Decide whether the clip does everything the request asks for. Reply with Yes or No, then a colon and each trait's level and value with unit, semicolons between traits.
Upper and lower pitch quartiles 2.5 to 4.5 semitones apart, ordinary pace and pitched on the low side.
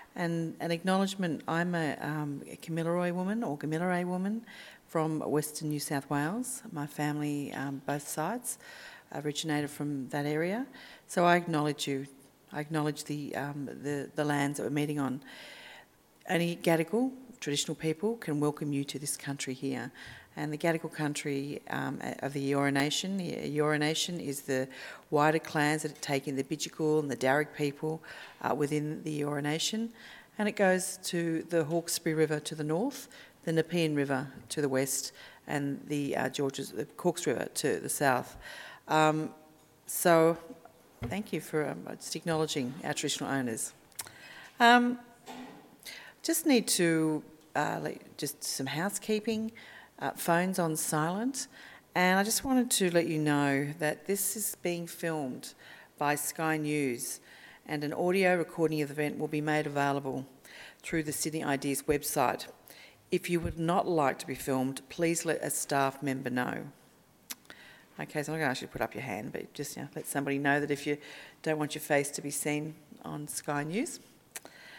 No: average, 2.9 semitones; average, 165 wpm; medium, 155 Hz